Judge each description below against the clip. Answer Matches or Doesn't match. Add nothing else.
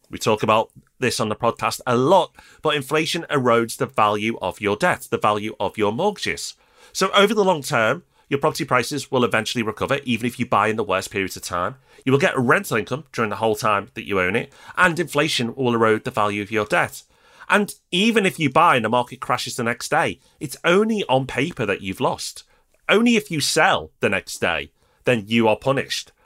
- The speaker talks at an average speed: Doesn't match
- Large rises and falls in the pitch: Matches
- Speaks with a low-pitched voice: Matches